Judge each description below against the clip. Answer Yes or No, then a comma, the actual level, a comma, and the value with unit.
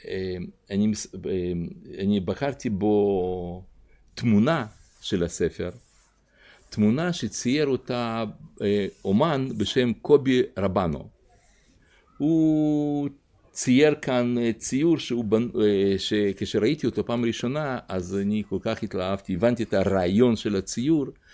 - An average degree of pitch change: Yes, average, 4.5 semitones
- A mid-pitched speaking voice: No, low, 110 Hz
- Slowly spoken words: Yes, slow, 95 wpm